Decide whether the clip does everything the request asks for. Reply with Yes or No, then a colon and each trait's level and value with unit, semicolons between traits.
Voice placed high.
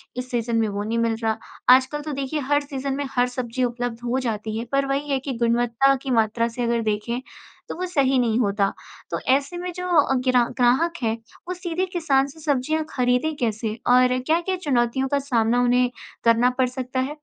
Yes: very high, 255 Hz